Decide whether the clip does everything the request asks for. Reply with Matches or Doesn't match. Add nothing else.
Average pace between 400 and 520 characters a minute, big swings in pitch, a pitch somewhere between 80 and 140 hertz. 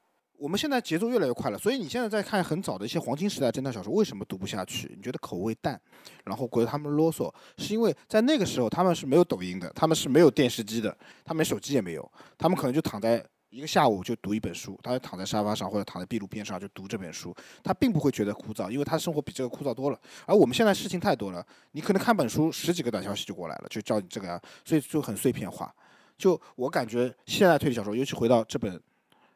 Matches